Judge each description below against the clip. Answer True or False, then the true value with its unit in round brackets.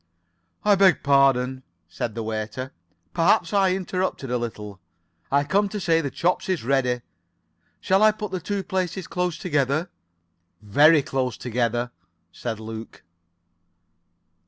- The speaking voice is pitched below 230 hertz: True (140 Hz)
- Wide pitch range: True (7.1 semitones)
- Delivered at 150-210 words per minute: False (135 wpm)